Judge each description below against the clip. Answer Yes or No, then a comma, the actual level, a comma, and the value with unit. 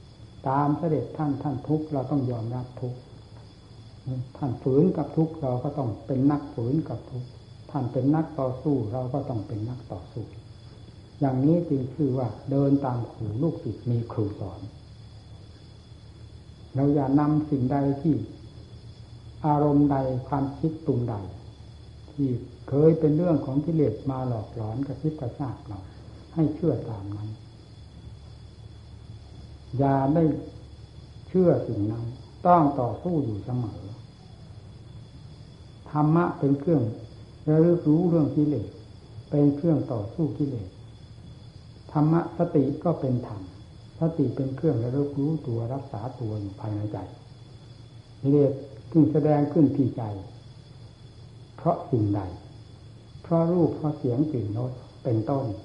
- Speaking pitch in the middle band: No, low, 125 Hz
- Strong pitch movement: No, average, 4.5 semitones